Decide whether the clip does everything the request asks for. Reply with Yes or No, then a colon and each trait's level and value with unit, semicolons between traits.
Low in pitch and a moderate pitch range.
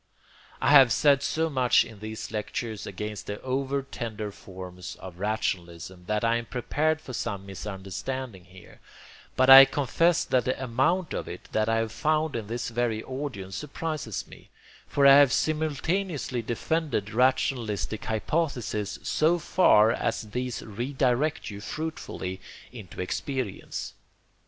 Yes: low, 120 Hz; average, 4.9 semitones